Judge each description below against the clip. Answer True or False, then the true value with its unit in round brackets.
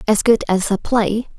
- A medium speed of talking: False (215 wpm)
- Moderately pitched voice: False (215 Hz)